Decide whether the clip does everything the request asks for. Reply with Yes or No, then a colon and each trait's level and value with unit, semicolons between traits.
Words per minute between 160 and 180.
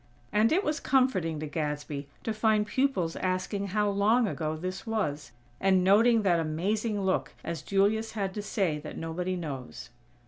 Yes: average, 165 wpm